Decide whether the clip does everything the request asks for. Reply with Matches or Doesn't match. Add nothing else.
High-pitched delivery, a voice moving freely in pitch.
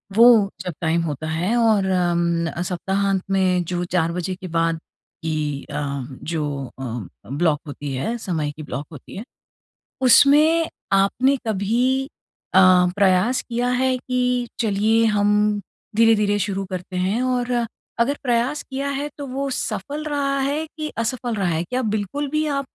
Matches